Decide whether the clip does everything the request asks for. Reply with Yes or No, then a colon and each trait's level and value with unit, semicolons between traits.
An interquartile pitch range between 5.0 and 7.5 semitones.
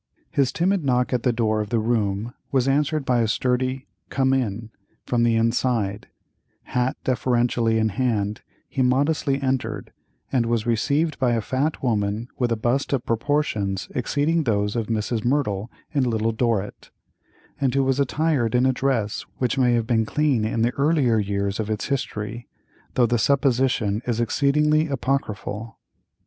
No: average, 3.5 semitones